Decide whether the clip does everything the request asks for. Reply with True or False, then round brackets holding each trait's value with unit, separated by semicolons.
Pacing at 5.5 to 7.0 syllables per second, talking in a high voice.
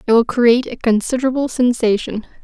True (6.1 syllables/s; 240 Hz)